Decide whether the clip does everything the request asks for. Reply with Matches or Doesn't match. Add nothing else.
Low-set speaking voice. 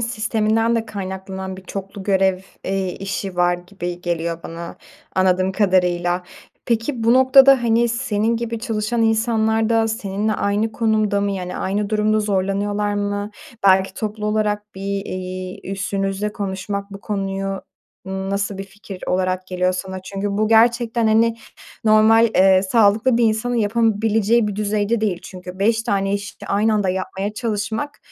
Doesn't match